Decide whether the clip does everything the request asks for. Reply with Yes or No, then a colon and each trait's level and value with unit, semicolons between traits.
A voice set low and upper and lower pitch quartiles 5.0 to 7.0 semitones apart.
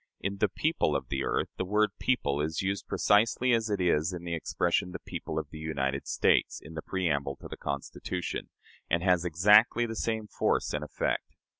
Yes: very low, 90 Hz; average, 5.3 semitones